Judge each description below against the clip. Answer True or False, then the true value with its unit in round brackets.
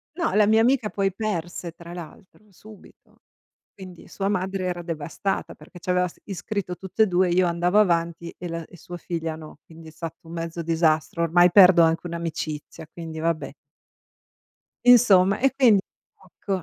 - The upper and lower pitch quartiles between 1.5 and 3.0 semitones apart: True (2.7 semitones)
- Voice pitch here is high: False (175 Hz)